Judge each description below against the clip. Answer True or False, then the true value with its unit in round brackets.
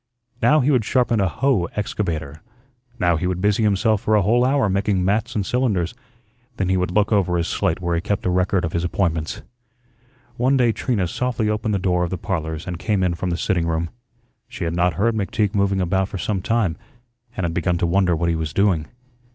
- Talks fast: True (220 wpm)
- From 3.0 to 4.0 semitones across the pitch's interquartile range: True (3.7 semitones)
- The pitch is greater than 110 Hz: False (95 Hz)